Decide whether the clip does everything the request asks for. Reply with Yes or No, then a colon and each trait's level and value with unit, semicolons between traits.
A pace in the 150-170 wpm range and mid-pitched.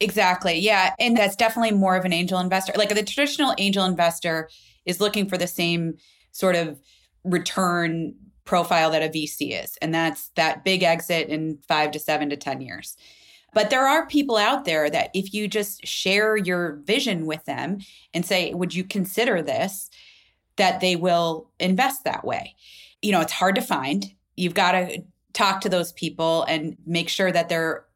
No: average, 180 wpm; medium, 180 Hz